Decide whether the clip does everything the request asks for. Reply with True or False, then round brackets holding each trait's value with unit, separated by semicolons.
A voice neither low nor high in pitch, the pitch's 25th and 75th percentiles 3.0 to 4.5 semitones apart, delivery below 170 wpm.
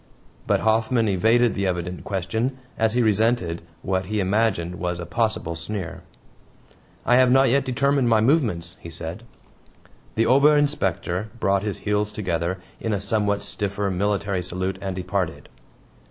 False (100 Hz; 3.8 semitones; 150 wpm)